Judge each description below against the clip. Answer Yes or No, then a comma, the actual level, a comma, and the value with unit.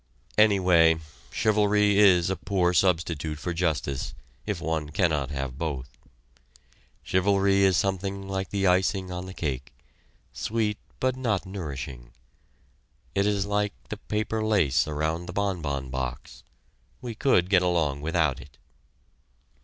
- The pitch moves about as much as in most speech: Yes, average, 4.6 semitones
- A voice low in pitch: Yes, very low, 90 Hz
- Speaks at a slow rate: Yes, slow, 130 wpm